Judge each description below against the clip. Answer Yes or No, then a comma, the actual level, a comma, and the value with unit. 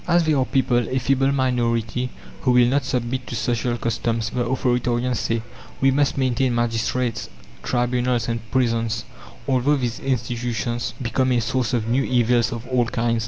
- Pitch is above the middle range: No, low, 120 Hz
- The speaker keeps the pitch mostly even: Yes, narrow, 1.8 semitones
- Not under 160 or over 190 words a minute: Yes, average, 165 wpm